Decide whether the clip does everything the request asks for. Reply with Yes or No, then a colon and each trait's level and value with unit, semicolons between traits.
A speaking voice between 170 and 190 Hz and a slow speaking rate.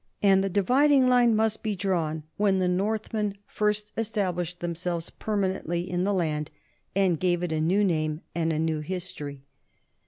No: medium, 185 Hz; average, 160 wpm